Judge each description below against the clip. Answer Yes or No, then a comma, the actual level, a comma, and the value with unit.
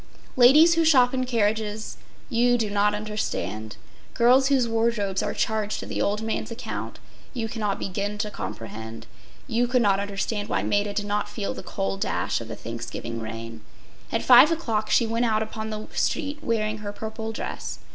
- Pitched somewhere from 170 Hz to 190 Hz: No, high, 215 Hz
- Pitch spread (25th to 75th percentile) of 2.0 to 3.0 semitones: Yes, average, 2.7 semitones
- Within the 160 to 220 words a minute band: Yes, average, 175 wpm